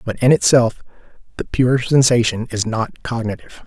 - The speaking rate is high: No, average, 145 wpm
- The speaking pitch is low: Yes, low, 120 Hz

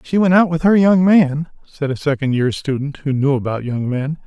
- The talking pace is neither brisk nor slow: No, fast, 240 wpm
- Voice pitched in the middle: Yes, medium, 150 Hz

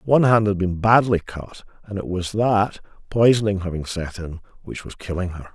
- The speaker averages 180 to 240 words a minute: Yes, average, 195 wpm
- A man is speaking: Yes, male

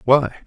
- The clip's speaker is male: Yes, male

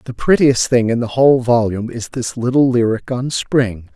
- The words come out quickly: No, average, 195 wpm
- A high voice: No, low, 120 Hz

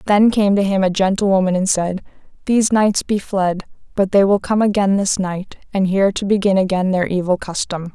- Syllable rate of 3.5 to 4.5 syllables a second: No, 5.4 syllables/s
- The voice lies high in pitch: Yes, high, 195 Hz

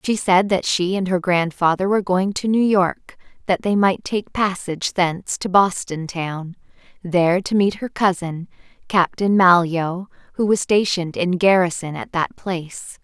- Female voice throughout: Yes, female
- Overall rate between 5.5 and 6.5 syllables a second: No, 4.5 syllables/s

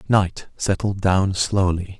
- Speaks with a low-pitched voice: Yes, very low, 95 Hz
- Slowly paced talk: Yes, slow, 120 wpm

